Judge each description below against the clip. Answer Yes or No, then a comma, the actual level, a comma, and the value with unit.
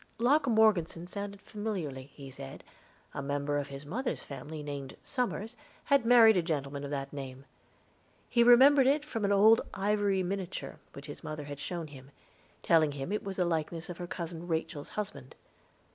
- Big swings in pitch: Yes, wide, 6.7 semitones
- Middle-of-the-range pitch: Yes, medium, 170 Hz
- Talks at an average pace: Yes, average, 175 wpm